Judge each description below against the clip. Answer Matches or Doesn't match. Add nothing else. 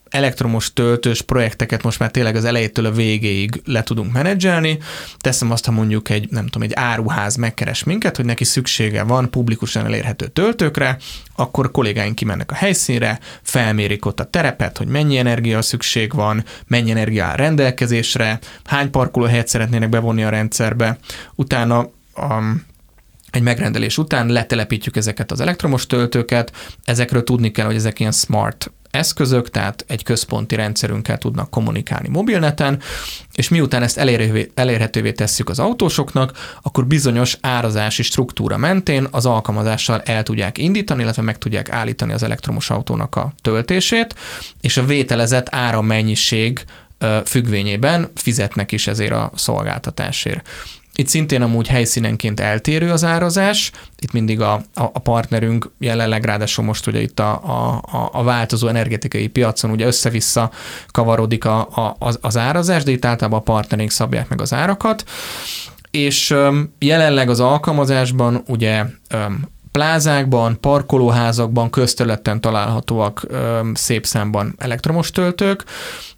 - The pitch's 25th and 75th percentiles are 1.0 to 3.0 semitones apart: Doesn't match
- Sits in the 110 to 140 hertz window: Matches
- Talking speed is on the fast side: Doesn't match